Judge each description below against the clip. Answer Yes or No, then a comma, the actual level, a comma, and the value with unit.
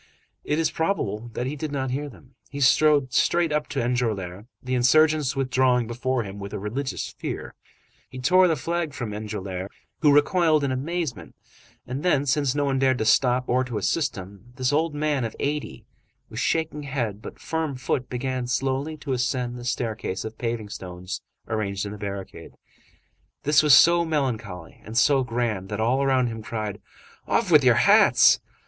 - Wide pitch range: No, average, 4.9 semitones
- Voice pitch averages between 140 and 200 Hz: No, low, 130 Hz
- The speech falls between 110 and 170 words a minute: No, average, 180 wpm